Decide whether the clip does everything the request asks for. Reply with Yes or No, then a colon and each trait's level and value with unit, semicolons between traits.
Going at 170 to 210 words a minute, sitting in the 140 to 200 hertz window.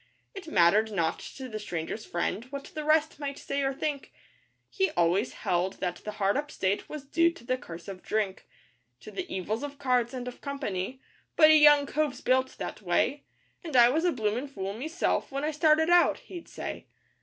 No: average, 200 wpm; very high, 260 Hz